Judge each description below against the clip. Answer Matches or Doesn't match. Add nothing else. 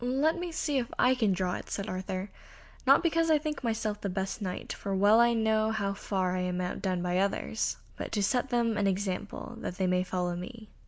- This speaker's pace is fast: Matches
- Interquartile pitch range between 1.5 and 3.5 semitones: Doesn't match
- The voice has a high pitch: Matches